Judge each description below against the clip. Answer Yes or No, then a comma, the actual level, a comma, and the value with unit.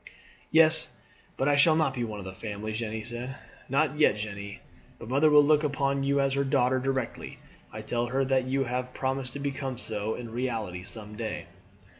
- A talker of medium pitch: No, low, 130 Hz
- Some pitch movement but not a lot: Yes, average, 3.8 semitones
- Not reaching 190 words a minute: No, average, 195 wpm